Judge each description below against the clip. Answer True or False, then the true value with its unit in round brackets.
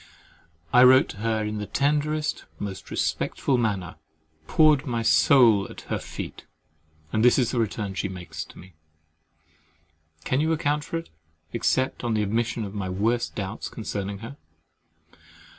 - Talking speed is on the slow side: False (150 wpm)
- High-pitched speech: False (115 Hz)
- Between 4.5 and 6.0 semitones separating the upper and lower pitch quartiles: True (4.8 semitones)